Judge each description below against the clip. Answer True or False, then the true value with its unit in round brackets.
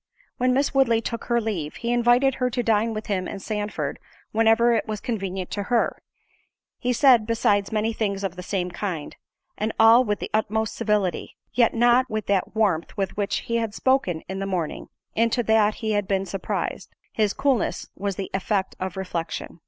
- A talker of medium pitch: False (215 Hz)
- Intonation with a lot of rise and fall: False (3.1 semitones)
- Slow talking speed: False (185 wpm)